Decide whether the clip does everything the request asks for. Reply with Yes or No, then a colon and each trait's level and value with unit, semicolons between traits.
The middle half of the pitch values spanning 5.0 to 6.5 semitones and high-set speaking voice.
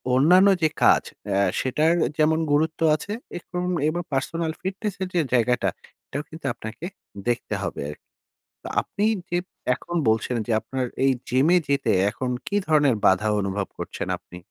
No: wide, 5.6 semitones; medium, 145 Hz